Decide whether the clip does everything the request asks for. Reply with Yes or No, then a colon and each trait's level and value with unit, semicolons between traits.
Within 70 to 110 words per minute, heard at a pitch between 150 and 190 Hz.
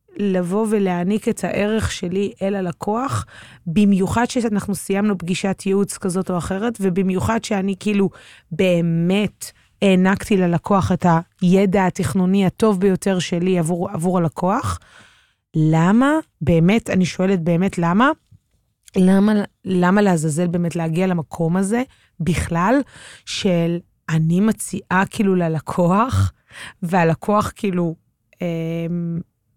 Yes: average, 105 wpm; medium, 185 Hz